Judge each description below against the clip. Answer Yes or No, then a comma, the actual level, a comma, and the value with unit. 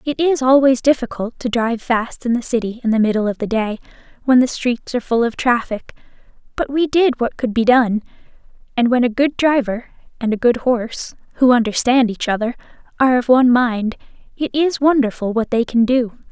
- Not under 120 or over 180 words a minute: No, average, 200 wpm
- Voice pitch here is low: No, high, 245 Hz